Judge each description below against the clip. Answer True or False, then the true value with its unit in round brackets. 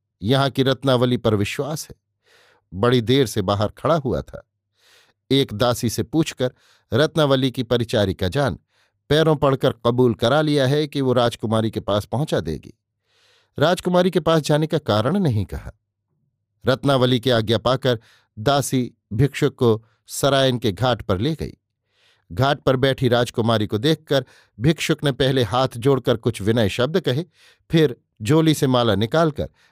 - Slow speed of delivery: False (155 wpm)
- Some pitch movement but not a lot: True (4.2 semitones)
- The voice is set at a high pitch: False (125 Hz)